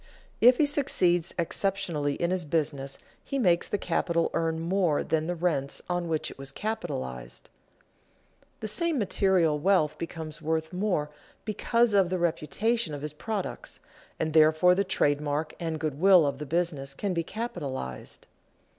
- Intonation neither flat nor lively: Yes, average, 4.3 semitones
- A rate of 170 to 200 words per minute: No, average, 155 wpm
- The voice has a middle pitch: Yes, medium, 165 Hz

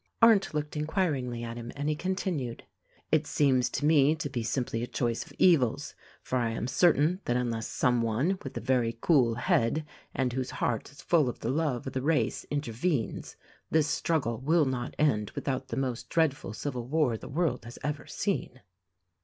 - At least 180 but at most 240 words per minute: Yes, average, 185 wpm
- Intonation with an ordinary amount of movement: Yes, average, 4.2 semitones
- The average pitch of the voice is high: No, low, 130 Hz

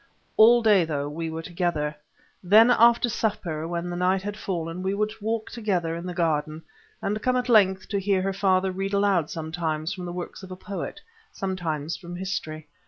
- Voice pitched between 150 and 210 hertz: Yes, medium, 185 Hz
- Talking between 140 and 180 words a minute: No, average, 190 wpm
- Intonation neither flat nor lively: Yes, average, 3.5 semitones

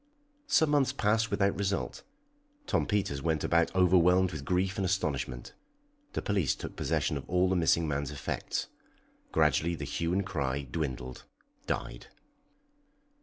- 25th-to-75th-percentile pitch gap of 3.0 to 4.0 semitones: No, average, 5.0 semitones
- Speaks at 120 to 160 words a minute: Yes, average, 140 wpm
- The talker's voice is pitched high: No, very low, 85 Hz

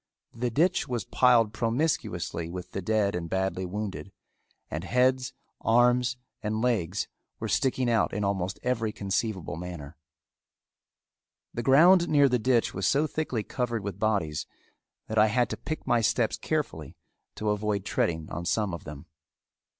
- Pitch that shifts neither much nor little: Yes, average, 4.7 semitones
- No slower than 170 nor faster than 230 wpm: No, average, 150 wpm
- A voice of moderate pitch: No, low, 110 Hz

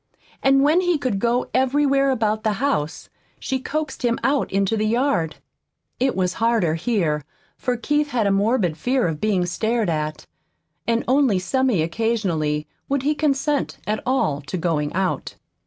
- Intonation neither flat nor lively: No, wide, 6.7 semitones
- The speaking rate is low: No, average, 160 wpm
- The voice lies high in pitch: Yes, high, 230 Hz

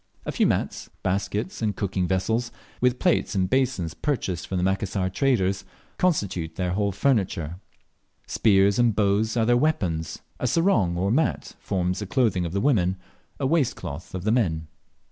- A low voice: Yes, low, 100 Hz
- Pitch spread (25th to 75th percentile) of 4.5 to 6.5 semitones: Yes, average, 4.9 semitones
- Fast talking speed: No, average, 165 wpm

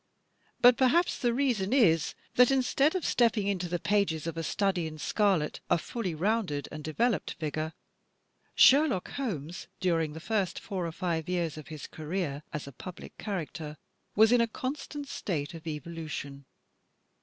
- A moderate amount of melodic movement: No, wide, 6.5 semitones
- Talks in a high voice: No, medium, 180 Hz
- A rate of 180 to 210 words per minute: No, average, 160 wpm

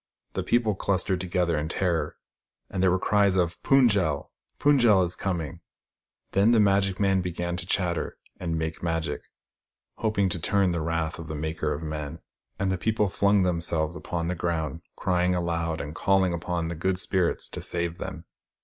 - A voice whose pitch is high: No, very low, 90 Hz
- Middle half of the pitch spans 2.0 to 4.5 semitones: Yes, narrow, 2.6 semitones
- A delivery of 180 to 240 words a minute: Yes, average, 195 wpm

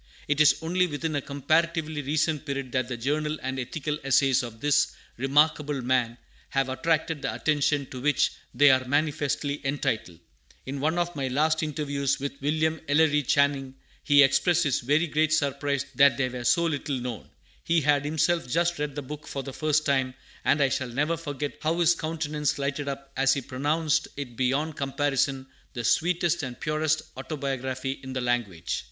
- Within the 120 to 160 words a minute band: No, average, 175 wpm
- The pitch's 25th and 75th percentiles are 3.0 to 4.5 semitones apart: No, narrow, 2.6 semitones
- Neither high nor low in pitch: Yes, medium, 145 Hz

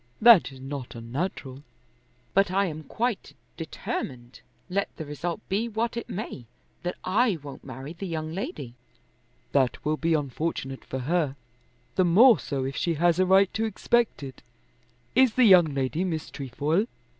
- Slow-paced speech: No, average, 165 wpm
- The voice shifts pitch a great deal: Yes, wide, 6.1 semitones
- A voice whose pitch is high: No, medium, 165 Hz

